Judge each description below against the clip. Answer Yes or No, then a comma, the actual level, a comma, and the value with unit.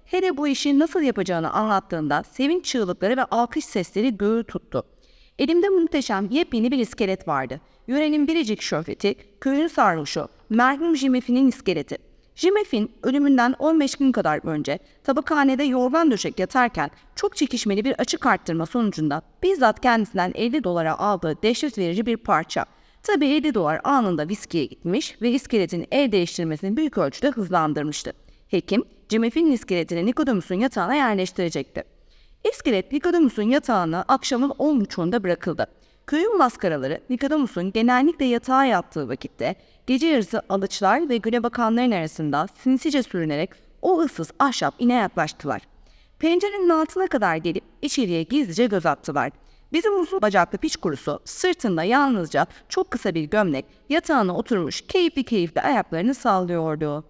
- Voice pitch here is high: Yes, high, 240 Hz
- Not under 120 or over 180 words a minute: Yes, average, 130 wpm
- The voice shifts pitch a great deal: Yes, wide, 7.4 semitones